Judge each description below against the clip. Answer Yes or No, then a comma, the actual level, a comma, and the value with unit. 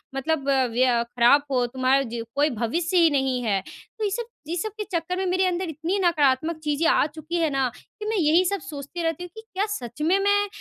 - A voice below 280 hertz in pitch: No, very high, 315 Hz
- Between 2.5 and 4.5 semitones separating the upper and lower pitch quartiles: No, average, 5.3 semitones